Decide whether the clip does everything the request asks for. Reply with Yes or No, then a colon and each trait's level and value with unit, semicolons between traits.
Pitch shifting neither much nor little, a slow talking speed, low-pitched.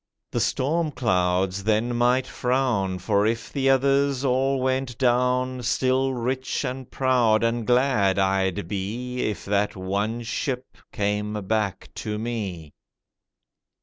Yes: average, 4.2 semitones; slow, 125 wpm; low, 120 Hz